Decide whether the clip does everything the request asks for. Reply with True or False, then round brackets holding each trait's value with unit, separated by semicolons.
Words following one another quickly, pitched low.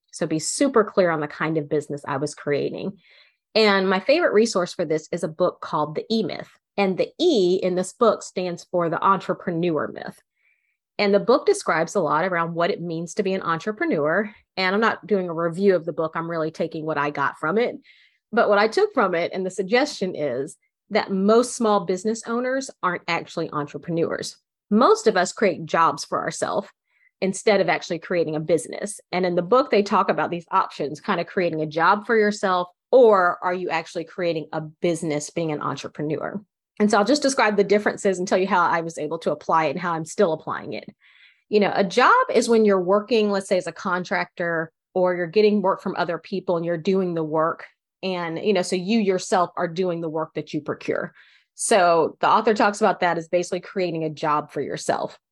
False (215 wpm; 185 Hz)